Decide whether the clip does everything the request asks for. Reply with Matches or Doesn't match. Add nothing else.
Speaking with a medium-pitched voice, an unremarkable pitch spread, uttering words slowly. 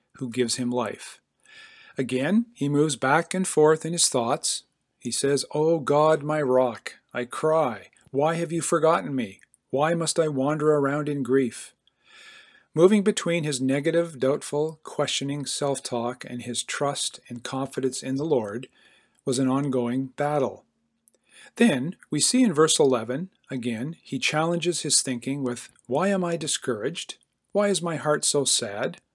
Doesn't match